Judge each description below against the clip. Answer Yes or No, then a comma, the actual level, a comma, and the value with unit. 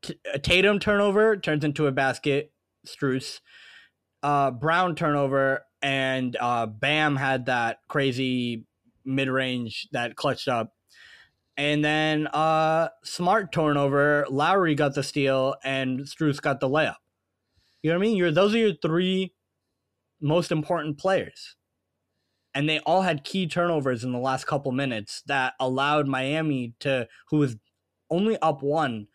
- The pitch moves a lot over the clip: No, average, 3.5 semitones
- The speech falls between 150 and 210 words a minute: No, average, 140 wpm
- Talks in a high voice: No, medium, 140 Hz